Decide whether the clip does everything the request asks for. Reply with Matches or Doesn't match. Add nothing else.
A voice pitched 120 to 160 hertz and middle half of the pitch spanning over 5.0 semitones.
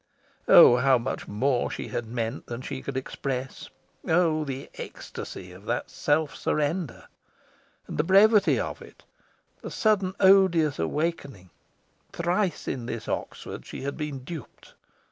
Matches